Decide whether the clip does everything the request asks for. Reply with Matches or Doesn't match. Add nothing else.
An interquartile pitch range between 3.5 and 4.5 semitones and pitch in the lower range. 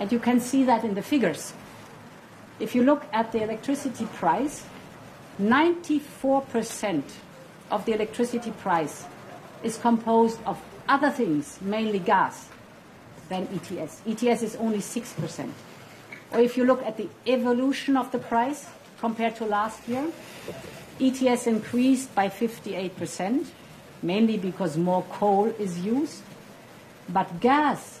Doesn't match